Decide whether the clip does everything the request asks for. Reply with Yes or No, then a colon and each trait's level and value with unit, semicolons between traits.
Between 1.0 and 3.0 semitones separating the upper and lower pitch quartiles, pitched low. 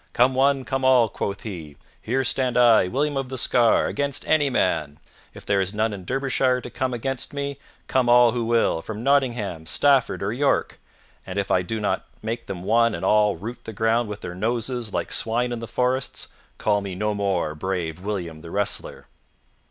No: average, 4.5 semitones; low, 115 Hz